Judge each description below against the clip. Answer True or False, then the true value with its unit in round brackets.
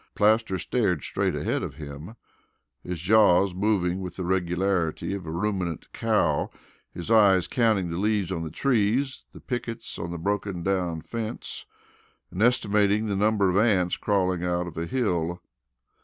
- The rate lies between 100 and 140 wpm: False (155 wpm)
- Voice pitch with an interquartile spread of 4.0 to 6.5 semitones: False (3.5 semitones)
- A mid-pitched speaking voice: False (95 Hz)